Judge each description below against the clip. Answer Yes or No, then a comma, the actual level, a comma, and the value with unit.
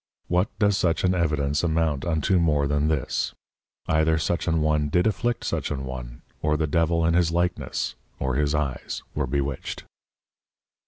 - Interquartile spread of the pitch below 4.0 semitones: Yes, average, 2.9 semitones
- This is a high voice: No, very low, 80 Hz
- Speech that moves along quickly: No, average, 165 wpm